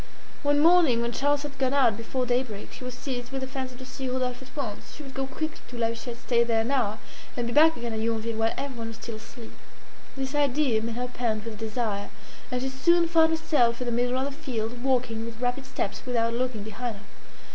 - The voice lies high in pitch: Yes, very high, 250 Hz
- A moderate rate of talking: No, fast, 235 wpm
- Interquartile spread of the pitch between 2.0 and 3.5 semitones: Yes, average, 2.8 semitones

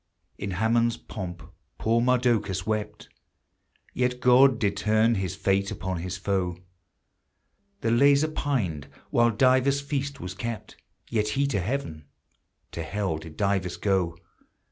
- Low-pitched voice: Yes, low, 105 Hz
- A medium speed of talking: No, slow, 130 wpm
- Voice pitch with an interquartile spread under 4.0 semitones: No, average, 4.9 semitones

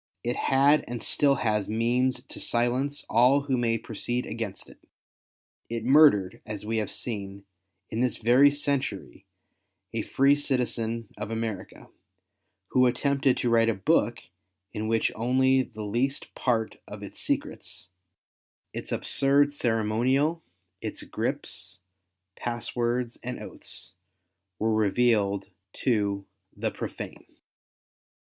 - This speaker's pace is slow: Yes, slow, 130 wpm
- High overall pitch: No, low, 120 Hz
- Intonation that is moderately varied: Yes, average, 3.3 semitones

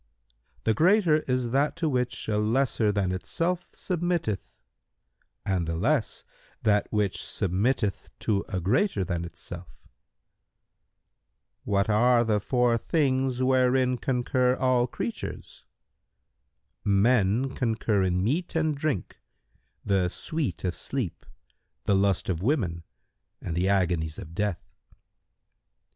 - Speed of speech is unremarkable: No, slow, 120 wpm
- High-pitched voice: No, low, 110 Hz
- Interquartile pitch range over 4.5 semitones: Yes, wide, 5.4 semitones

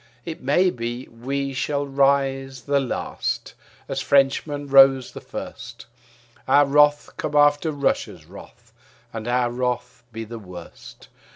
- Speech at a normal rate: No, slow, 130 wpm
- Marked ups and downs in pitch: No, narrow, 2.6 semitones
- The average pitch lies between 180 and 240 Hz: No, low, 135 Hz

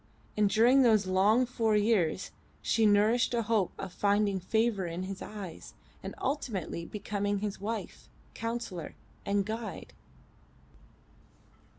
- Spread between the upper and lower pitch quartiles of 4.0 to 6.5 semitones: No, average, 2.8 semitones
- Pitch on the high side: Yes, high, 210 Hz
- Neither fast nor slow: No, slow, 120 wpm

